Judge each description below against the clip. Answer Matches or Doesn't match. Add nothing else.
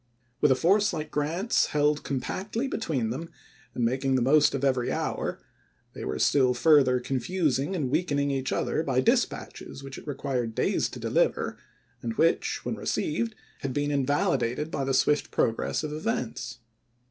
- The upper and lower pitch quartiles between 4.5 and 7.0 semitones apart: Doesn't match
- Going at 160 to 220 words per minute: Matches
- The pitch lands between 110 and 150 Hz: Matches